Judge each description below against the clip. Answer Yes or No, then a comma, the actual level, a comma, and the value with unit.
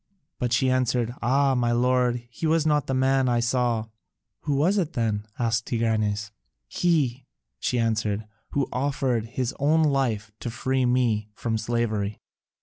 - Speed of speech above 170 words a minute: No, average, 150 wpm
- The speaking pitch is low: Yes, low, 125 Hz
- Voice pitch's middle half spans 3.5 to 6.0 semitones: No, average, 2.9 semitones